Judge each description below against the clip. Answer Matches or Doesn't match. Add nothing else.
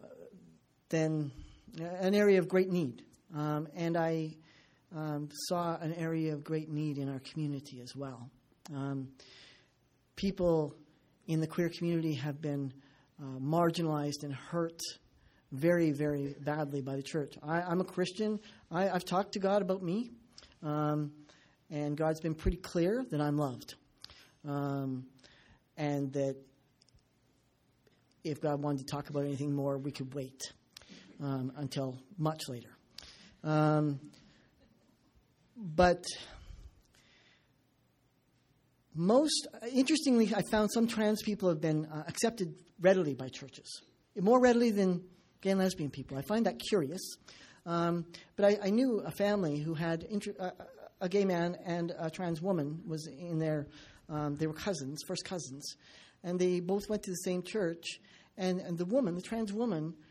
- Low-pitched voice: Doesn't match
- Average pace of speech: Matches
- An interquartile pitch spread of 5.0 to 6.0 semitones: Doesn't match